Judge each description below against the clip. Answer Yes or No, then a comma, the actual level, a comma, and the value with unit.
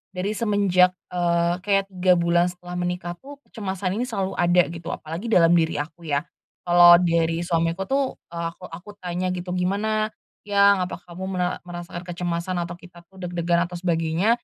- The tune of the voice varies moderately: No, narrow, 1.8 semitones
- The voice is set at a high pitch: No, medium, 180 Hz